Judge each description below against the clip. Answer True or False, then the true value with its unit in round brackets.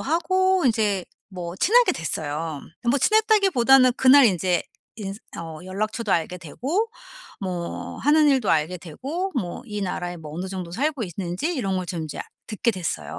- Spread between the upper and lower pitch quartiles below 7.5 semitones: False (7.9 semitones)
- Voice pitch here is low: False (200 Hz)